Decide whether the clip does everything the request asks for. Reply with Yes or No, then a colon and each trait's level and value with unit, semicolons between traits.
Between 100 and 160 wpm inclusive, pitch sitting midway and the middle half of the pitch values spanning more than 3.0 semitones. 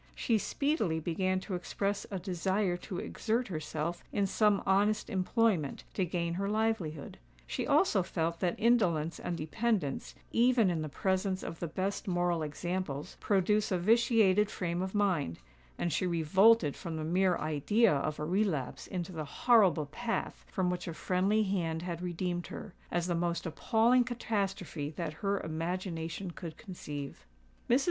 Yes: average, 155 wpm; medium, 180 Hz; average, 3.9 semitones